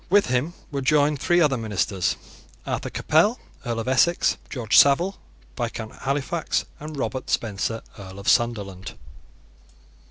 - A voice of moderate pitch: No, low, 130 Hz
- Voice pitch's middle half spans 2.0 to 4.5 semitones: No, average, 5.3 semitones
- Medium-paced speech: No, slow, 130 wpm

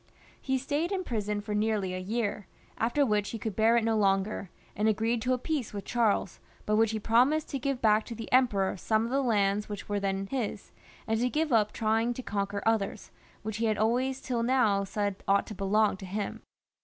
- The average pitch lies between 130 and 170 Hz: No, high, 220 Hz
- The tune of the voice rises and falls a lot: No, average, 3.0 semitones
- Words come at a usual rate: No, fast, 215 wpm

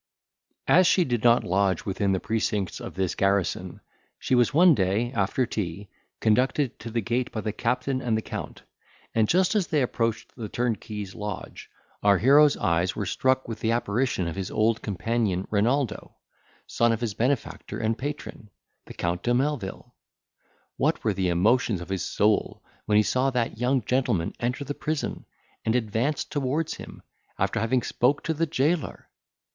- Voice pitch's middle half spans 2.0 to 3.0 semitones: No, average, 4.3 semitones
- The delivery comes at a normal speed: Yes, average, 170 wpm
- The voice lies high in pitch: No, low, 115 Hz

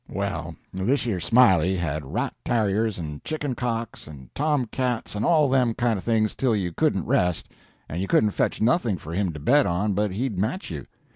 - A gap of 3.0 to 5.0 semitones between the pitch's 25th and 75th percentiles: No, wide, 5.5 semitones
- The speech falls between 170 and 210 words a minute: Yes, average, 195 wpm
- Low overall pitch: Yes, low, 105 Hz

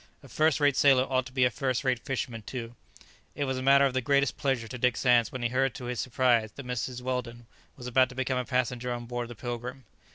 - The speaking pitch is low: Yes, low, 125 Hz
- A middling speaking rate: No, fast, 250 wpm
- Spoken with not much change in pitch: Yes, narrow, 1.6 semitones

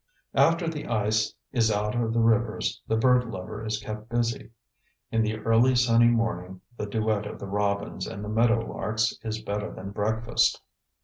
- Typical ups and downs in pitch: No, narrow, 1.8 semitones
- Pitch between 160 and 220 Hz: No, low, 110 Hz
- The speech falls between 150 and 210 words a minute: Yes, average, 175 wpm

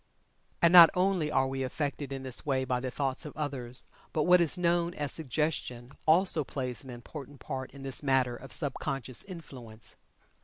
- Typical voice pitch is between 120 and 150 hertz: Yes, low, 135 Hz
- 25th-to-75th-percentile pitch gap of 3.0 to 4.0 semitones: Yes, average, 3.5 semitones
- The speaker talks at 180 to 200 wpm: Yes, average, 185 wpm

